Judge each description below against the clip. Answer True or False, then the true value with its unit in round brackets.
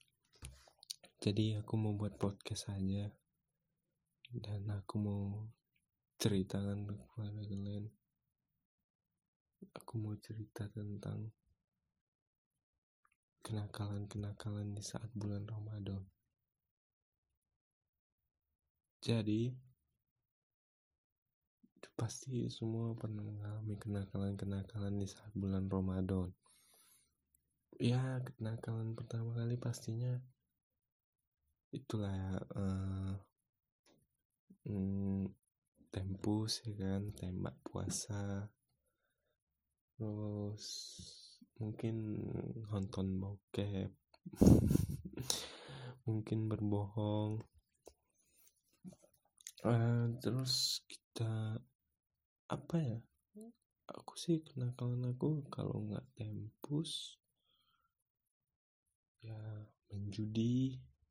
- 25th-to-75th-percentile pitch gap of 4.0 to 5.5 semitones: False (2.9 semitones)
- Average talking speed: False (60 wpm)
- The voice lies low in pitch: True (105 Hz)